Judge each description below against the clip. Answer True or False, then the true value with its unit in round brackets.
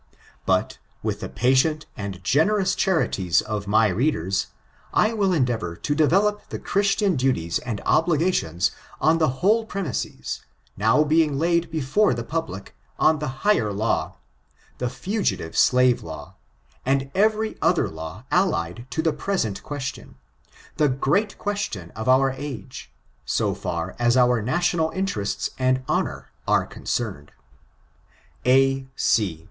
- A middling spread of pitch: False (7.5 semitones)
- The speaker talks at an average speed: False (130 wpm)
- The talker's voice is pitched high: False (135 Hz)